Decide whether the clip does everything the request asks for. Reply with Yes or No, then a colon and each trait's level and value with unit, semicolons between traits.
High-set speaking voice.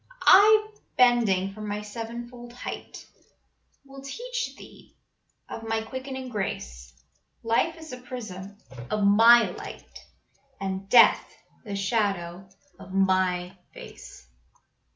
Yes: high, 220 Hz